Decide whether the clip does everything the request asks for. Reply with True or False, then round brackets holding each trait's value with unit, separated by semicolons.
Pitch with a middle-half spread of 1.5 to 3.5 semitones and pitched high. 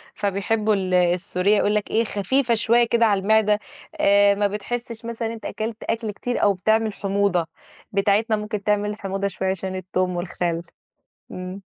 True (2.4 semitones; 205 Hz)